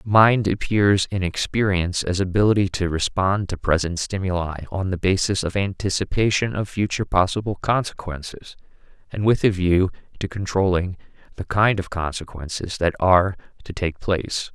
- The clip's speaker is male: Yes, male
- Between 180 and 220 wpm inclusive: No, average, 145 wpm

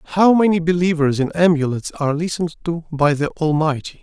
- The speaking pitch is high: No, medium, 160 Hz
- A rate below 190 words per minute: Yes, average, 165 wpm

